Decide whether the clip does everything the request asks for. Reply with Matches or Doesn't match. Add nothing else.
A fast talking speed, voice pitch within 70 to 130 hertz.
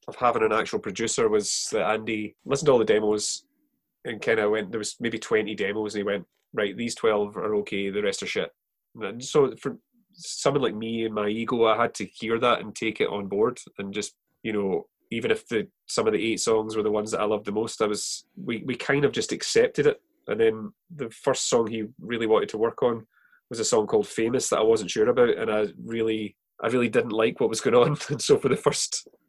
Matches